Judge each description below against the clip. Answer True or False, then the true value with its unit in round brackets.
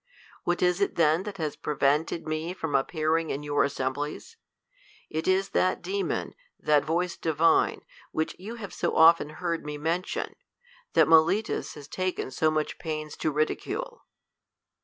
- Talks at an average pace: True (160 wpm)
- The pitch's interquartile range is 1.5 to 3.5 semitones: True (3.0 semitones)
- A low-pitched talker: False (160 Hz)